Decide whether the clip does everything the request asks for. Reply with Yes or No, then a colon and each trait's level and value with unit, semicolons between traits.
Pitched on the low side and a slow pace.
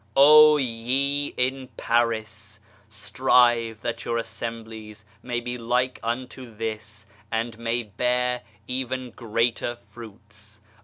Yes: low, 115 Hz; slow, 105 wpm